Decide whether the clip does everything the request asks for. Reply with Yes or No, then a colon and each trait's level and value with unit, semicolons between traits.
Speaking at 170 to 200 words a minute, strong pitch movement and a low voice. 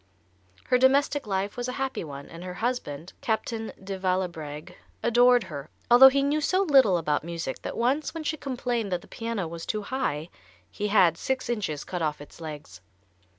No: average, 185 wpm; wide, 7.3 semitones; high, 205 Hz